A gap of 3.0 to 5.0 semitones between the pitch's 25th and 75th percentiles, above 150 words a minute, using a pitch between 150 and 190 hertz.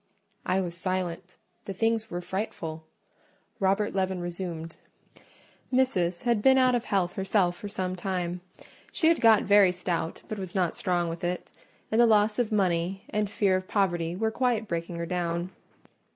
Yes: average, 3.3 semitones; average, 165 wpm; medium, 185 Hz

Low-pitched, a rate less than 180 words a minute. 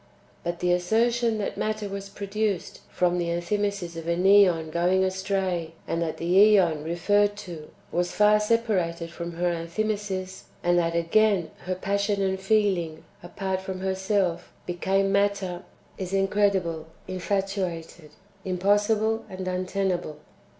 No: high, 190 Hz; slow, 135 wpm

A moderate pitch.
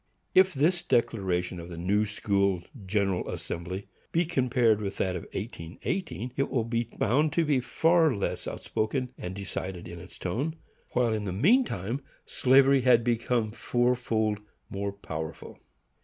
No: low, 110 Hz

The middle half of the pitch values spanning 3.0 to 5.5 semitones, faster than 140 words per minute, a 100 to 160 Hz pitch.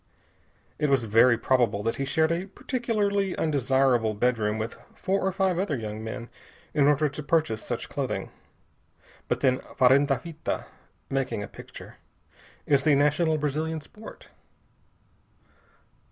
No: average, 4.9 semitones; slow, 135 wpm; medium, 140 Hz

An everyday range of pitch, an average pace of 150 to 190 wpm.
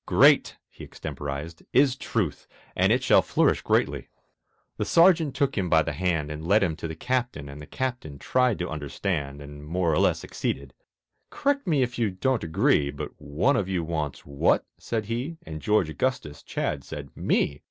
No: wide, 8.8 semitones; average, 185 wpm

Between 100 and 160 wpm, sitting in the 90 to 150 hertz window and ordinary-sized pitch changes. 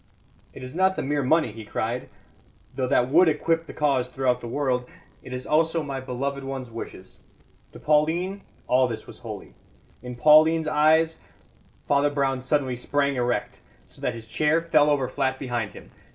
No: average, 180 wpm; medium, 140 Hz; average, 3.5 semitones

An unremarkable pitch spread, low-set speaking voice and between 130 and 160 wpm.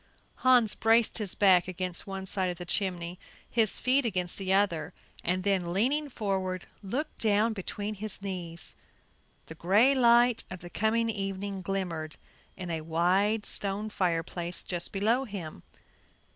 No: average, 3.5 semitones; high, 195 Hz; average, 145 wpm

